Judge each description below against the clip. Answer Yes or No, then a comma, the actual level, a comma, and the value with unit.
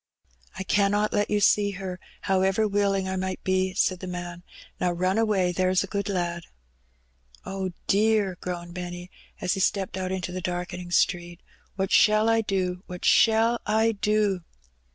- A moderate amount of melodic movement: No, narrow, 2.3 semitones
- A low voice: No, high, 190 Hz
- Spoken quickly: No, average, 165 wpm